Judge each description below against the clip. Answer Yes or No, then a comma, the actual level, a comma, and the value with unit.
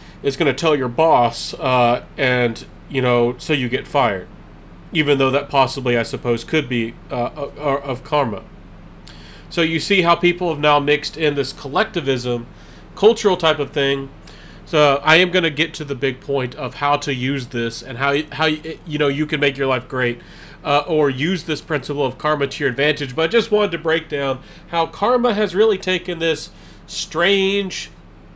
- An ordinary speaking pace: Yes, average, 195 wpm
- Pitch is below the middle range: No, medium, 145 Hz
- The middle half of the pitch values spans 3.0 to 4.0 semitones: Yes, average, 3.6 semitones